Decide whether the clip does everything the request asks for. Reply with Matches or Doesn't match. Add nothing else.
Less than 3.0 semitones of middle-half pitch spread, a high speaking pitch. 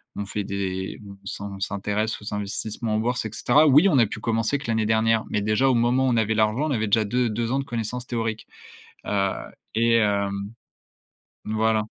Doesn't match